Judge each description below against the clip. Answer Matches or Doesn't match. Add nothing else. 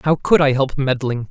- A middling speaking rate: Doesn't match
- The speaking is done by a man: Matches